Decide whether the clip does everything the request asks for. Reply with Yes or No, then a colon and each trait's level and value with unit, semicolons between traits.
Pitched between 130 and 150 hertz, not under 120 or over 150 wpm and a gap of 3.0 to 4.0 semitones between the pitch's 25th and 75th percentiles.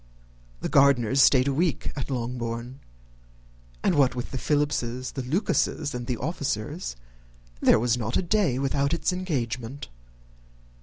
Yes: low, 135 Hz; average, 140 wpm; average, 3.3 semitones